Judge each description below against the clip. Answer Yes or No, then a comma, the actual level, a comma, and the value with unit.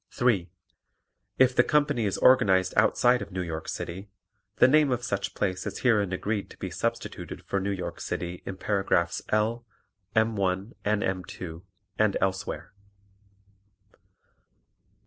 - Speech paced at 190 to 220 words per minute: No, average, 145 wpm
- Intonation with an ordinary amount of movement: Yes, average, 3.7 semitones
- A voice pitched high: No, low, 100 Hz